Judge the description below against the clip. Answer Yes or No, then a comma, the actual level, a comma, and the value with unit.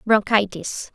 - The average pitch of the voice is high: Yes, high, 205 Hz